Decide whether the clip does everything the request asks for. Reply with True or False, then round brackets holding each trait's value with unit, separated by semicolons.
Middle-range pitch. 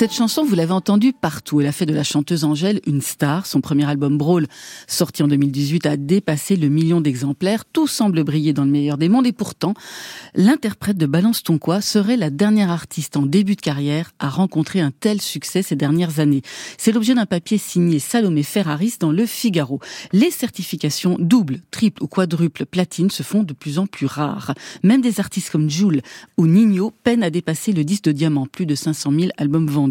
True (170 Hz)